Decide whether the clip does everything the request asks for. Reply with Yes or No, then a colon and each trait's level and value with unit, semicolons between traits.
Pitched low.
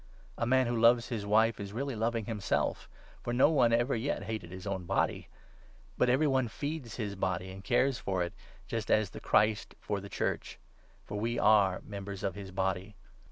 Yes: low, 110 Hz